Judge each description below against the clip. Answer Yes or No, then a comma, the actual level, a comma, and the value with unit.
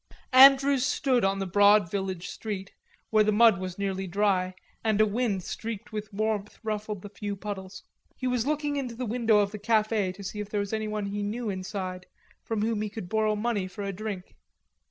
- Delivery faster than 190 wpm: Yes, average, 200 wpm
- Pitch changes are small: Yes, narrow, 2.2 semitones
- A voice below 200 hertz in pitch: No, high, 210 Hz